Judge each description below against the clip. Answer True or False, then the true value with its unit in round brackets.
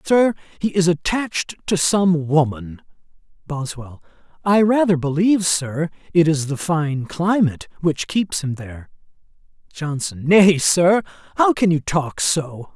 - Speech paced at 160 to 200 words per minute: False (135 wpm)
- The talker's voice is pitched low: False (165 Hz)